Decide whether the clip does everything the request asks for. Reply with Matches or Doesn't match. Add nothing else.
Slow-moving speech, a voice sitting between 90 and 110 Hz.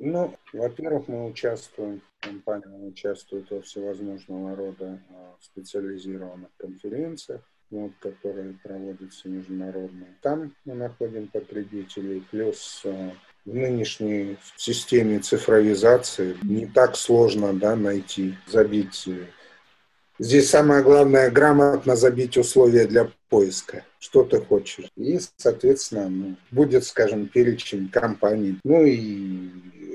Matches